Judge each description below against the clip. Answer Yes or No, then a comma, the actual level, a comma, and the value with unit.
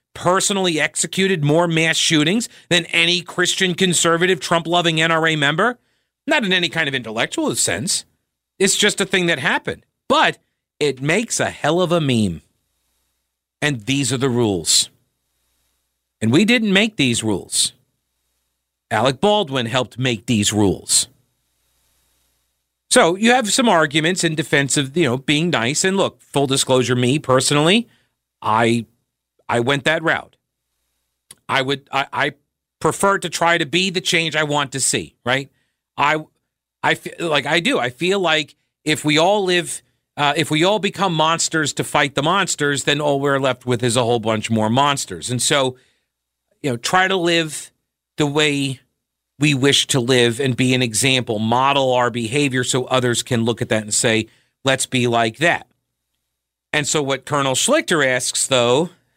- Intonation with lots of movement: Yes, wide, 6.1 semitones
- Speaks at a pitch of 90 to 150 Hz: Yes, medium, 140 Hz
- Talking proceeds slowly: No, average, 165 wpm